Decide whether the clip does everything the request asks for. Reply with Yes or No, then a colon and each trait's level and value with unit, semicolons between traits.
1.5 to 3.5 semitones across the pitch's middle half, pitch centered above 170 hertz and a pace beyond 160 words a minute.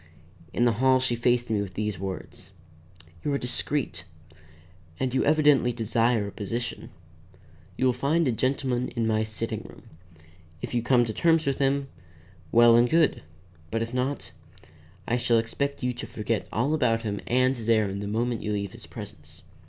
No: average, 2.9 semitones; low, 120 Hz; average, 175 wpm